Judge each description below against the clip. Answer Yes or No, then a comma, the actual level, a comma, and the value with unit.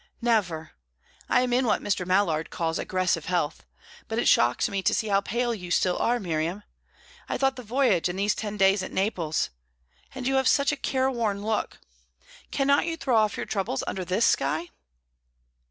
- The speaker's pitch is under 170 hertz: No, high, 205 Hz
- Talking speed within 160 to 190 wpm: Yes, average, 185 wpm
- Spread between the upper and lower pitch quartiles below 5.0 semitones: No, wide, 5.4 semitones